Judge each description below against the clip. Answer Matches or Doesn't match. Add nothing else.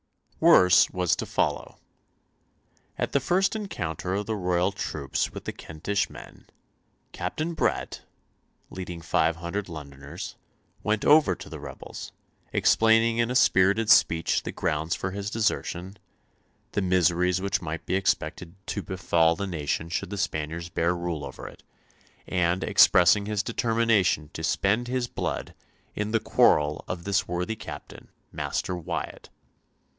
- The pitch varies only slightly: Doesn't match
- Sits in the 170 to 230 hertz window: Doesn't match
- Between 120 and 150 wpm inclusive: Matches